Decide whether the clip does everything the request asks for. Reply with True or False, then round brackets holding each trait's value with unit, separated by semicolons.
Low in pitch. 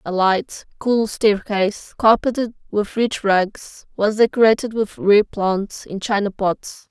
False (210 Hz)